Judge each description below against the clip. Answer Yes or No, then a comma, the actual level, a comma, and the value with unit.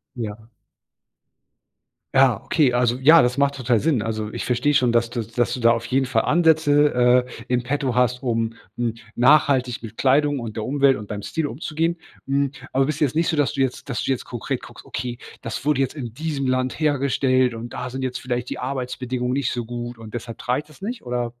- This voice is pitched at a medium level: No, low, 125 Hz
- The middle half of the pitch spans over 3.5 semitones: No, average, 2.7 semitones